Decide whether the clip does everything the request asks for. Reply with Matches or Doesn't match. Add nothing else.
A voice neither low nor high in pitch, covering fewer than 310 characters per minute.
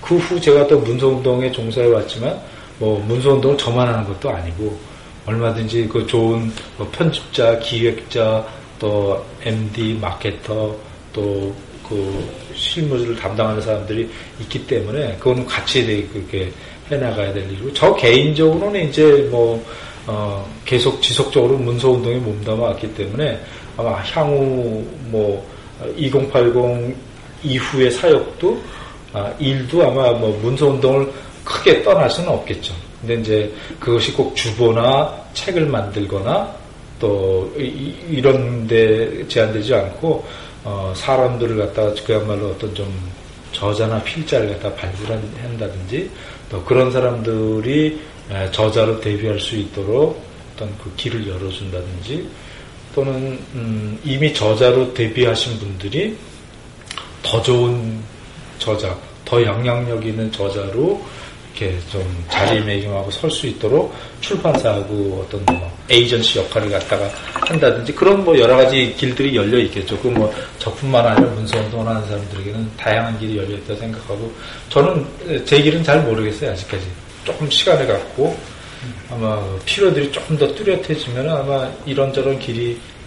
Doesn't match